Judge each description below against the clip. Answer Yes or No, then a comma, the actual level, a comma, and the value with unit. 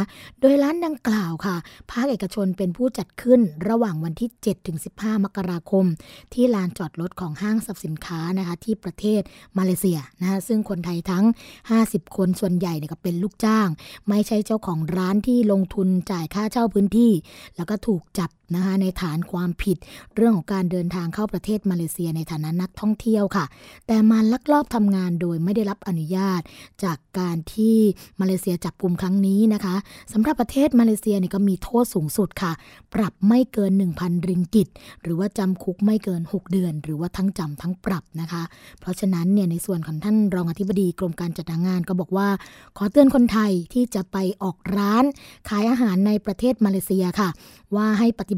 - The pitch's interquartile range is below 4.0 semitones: Yes, average, 3.1 semitones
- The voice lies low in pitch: No, high, 195 Hz